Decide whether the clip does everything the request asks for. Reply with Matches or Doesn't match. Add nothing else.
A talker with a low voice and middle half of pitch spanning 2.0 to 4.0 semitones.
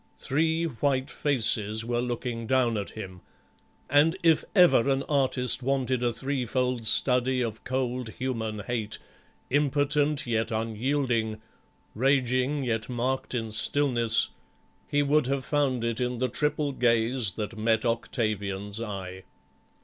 Matches